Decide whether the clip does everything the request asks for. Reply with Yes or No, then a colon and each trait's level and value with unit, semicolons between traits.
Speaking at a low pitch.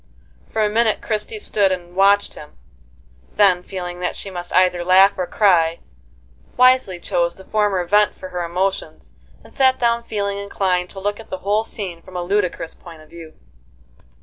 No: high, 190 Hz